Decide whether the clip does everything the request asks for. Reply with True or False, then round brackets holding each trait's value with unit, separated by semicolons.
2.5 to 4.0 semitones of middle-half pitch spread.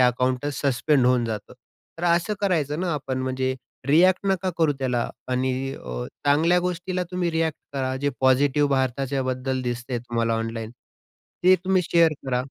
False (4.5 semitones)